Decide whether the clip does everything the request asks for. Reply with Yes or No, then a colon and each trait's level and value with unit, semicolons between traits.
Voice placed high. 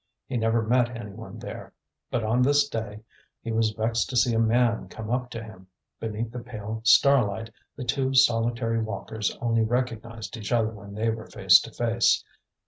No: low, 115 Hz